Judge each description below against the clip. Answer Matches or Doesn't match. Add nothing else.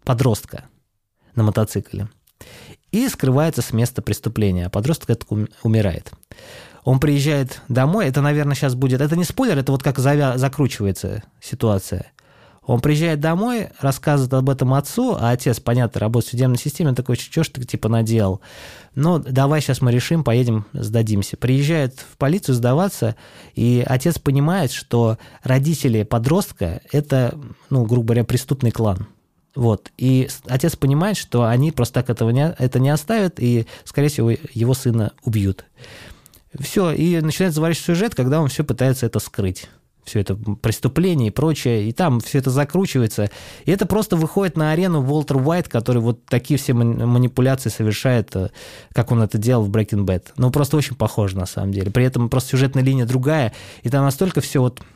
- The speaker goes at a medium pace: Doesn't match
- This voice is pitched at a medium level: Doesn't match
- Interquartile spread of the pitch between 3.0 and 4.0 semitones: Doesn't match